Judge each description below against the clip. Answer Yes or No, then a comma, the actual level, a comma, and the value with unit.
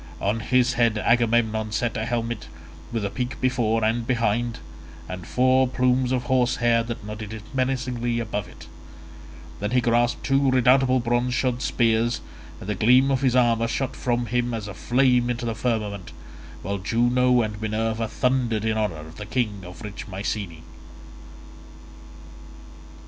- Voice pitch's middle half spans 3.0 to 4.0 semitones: No, narrow, 2.5 semitones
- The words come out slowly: No, average, 155 wpm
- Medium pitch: No, low, 120 Hz